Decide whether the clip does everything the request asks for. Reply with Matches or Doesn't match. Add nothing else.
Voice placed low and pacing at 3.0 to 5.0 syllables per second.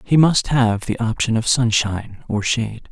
Matches